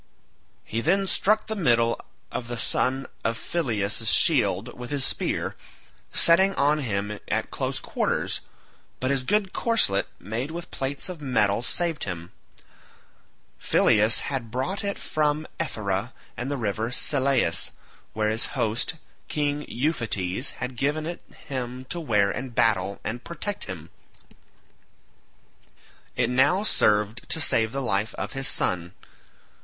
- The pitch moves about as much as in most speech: No, wide, 5.8 semitones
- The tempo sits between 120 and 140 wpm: Yes, slow, 135 wpm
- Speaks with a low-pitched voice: Yes, low, 125 Hz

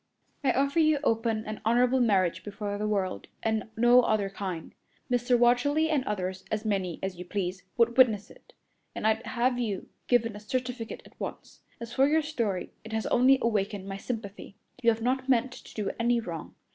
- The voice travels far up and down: No, average, 3.6 semitones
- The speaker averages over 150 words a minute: Yes, average, 190 wpm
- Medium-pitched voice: No, high, 225 Hz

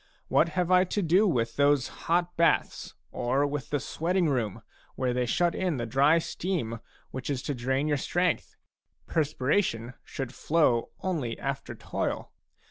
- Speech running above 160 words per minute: No, average, 155 wpm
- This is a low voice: No, medium, 145 Hz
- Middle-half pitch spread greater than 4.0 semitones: Yes, average, 5.2 semitones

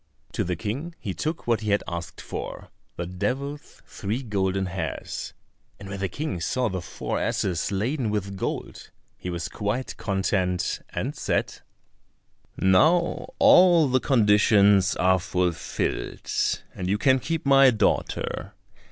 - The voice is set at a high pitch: No, low, 105 Hz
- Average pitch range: No, wide, 5.9 semitones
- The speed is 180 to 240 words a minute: No, average, 140 wpm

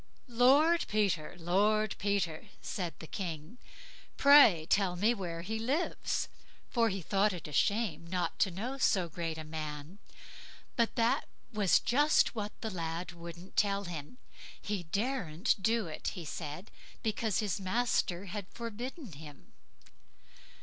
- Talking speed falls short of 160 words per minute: Yes, average, 140 wpm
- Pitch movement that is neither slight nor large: Yes, average, 4.9 semitones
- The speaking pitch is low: No, high, 195 Hz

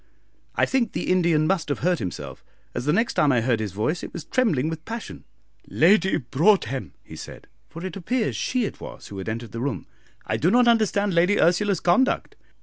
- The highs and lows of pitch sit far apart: Yes, wide, 7.4 semitones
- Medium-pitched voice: Yes, medium, 170 Hz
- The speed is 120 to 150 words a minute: No, fast, 205 wpm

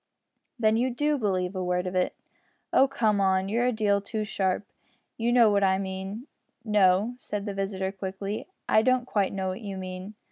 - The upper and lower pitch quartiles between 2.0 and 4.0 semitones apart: Yes, average, 2.8 semitones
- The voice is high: Yes, high, 200 Hz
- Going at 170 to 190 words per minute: Yes, average, 185 wpm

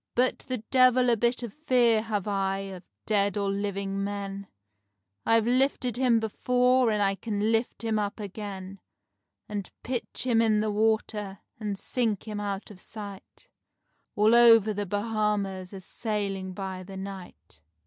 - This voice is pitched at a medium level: No, high, 210 Hz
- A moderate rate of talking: Yes, average, 155 wpm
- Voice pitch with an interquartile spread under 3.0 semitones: Yes, narrow, 2.5 semitones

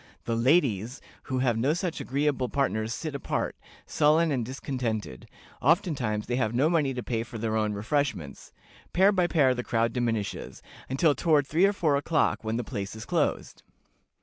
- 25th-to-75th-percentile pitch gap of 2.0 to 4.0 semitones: No, average, 4.9 semitones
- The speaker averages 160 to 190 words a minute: Yes, average, 175 wpm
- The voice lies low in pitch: Yes, low, 130 Hz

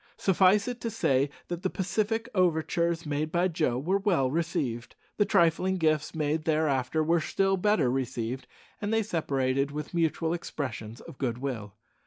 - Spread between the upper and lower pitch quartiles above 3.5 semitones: Yes, wide, 5.5 semitones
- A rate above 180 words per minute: No, average, 160 wpm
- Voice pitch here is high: No, medium, 160 Hz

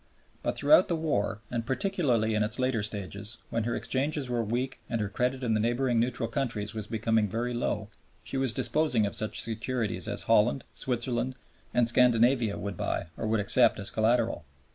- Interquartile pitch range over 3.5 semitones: No, average, 2.8 semitones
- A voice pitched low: Yes, low, 115 Hz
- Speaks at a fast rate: No, average, 185 wpm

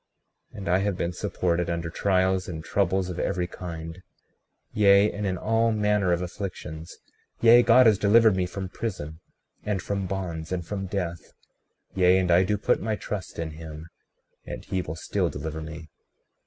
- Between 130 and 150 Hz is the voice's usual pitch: No, very low, 95 Hz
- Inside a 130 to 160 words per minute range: No, average, 175 wpm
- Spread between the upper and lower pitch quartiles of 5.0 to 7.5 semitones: No, average, 3.1 semitones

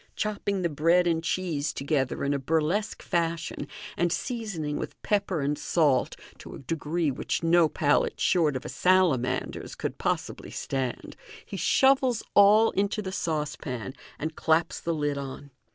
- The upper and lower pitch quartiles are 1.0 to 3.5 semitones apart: No, average, 4.3 semitones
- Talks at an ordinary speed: Yes, average, 150 wpm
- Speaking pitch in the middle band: Yes, medium, 165 Hz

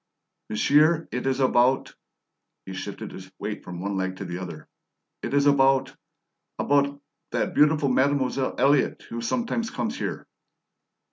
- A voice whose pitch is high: No, low, 135 Hz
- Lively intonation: Yes, wide, 6.1 semitones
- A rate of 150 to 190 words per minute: No, average, 140 wpm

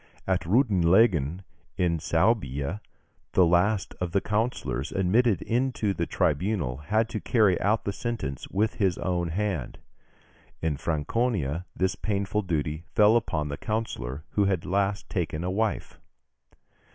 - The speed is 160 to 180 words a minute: No, slow, 135 wpm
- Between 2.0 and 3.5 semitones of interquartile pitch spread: No, average, 4.8 semitones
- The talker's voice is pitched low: Yes, very low, 95 Hz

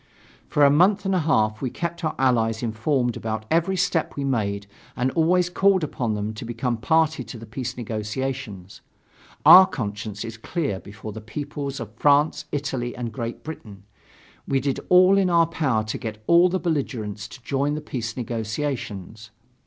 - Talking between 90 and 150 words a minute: No, average, 175 wpm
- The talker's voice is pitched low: Yes, low, 130 Hz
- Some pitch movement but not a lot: No, wide, 6.2 semitones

